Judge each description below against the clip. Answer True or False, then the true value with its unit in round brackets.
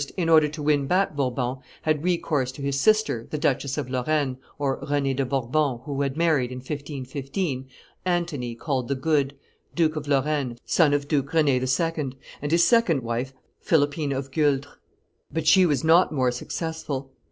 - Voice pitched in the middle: True (145 Hz)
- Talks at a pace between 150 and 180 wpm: True (165 wpm)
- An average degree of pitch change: True (3.0 semitones)